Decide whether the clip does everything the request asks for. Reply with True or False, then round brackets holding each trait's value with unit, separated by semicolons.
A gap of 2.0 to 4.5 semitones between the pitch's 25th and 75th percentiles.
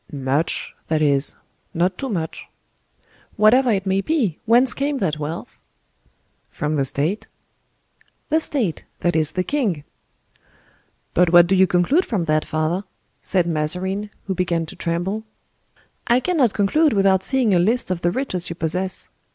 False (5.1 semitones)